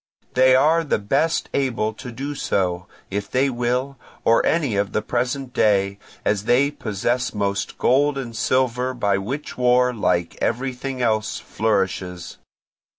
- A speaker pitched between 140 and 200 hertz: No, low, 125 Hz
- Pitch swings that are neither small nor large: Yes, average, 4.4 semitones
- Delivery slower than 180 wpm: Yes, average, 145 wpm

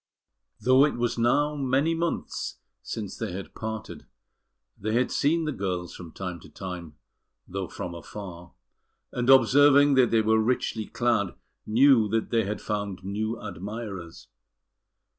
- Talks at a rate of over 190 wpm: No, average, 140 wpm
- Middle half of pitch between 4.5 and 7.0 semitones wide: Yes, average, 4.9 semitones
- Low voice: Yes, low, 110 Hz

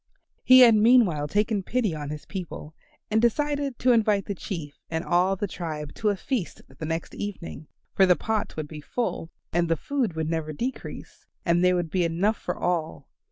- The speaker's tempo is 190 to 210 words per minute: Yes, average, 200 wpm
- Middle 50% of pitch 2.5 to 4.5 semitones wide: No, average, 5.3 semitones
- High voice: No, medium, 180 Hz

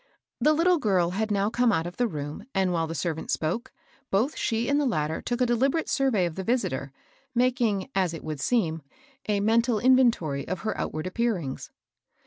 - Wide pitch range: Yes, wide, 6.5 semitones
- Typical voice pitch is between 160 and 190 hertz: No, high, 205 Hz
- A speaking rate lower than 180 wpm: No, average, 195 wpm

